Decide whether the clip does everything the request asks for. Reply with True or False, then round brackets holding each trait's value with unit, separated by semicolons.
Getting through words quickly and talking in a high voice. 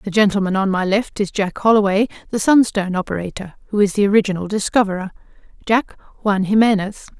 False (160 wpm; 205 Hz)